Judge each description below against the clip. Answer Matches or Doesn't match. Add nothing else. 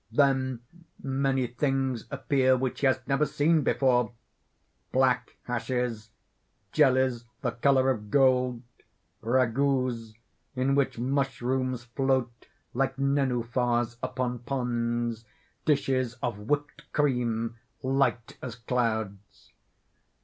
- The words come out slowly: Matches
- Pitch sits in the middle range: Doesn't match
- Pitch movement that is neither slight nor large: Doesn't match